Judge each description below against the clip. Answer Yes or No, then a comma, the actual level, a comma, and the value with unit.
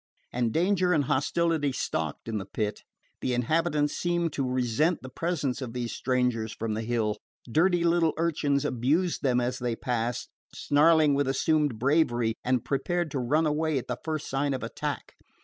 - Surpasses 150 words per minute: Yes, average, 170 wpm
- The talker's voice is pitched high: No, medium, 140 Hz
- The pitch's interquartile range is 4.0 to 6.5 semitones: Yes, average, 4.6 semitones